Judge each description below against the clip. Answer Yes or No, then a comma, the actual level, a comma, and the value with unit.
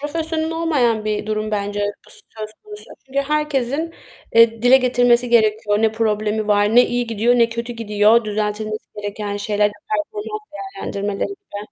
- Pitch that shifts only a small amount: No, average, 4.8 semitones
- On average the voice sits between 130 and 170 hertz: No, high, 230 Hz